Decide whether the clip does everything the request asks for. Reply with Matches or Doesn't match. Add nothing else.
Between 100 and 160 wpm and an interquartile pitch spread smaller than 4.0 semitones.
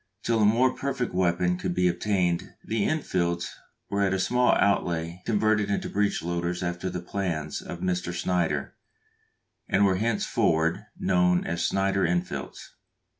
Matches